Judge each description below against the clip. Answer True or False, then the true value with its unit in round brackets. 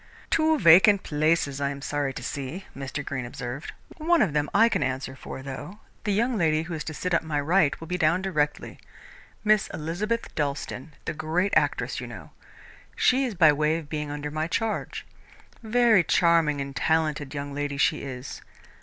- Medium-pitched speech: True (155 Hz)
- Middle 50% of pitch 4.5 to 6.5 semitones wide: True (4.9 semitones)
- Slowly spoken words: False (185 wpm)